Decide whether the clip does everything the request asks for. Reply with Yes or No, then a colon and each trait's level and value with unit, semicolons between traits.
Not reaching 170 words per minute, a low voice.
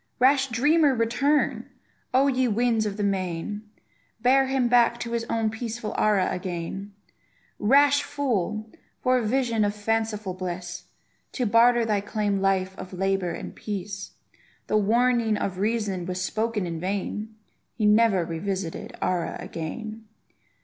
No: average, 140 wpm; high, 215 Hz